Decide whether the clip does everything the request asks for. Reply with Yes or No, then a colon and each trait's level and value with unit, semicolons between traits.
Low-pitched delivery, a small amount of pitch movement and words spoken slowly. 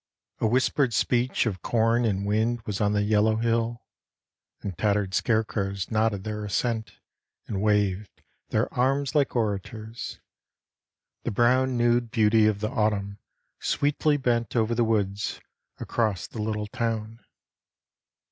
Yes: low, 110 Hz; narrow, 2.3 semitones; slow, 130 wpm